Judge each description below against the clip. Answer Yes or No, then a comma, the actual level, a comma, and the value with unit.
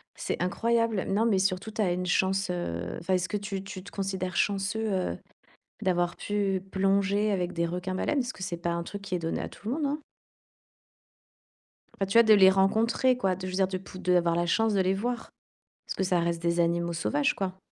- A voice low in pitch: No, high, 190 Hz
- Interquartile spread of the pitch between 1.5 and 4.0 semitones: Yes, narrow, 2.5 semitones